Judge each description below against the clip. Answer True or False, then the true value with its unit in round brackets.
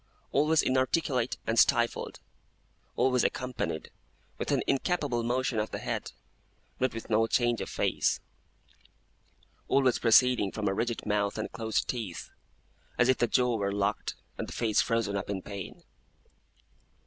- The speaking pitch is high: False (115 Hz)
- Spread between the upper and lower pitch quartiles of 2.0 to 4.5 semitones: True (3.1 semitones)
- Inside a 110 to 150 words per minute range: True (145 wpm)